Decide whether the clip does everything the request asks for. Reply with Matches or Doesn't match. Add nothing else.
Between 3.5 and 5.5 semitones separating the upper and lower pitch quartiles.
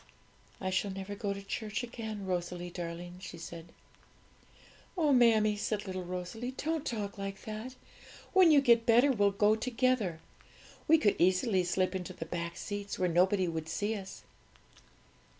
Matches